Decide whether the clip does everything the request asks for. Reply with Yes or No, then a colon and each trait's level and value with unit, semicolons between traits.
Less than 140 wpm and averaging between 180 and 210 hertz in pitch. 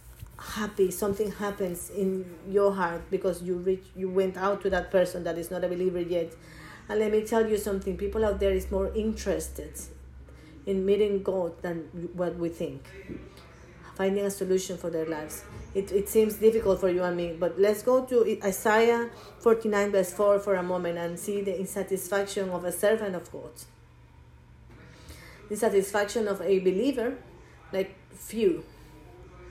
No: average, 165 wpm; high, 190 Hz